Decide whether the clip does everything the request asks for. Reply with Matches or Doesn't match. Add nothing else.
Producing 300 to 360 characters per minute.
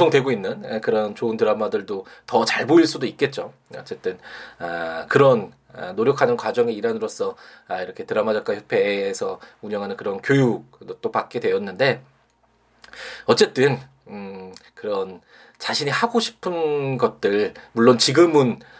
Doesn't match